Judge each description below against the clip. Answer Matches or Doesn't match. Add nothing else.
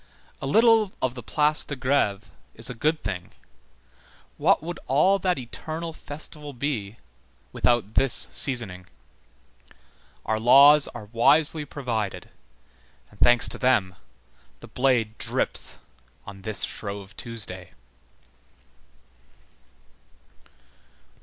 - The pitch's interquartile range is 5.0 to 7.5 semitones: Matches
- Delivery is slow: Matches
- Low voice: Matches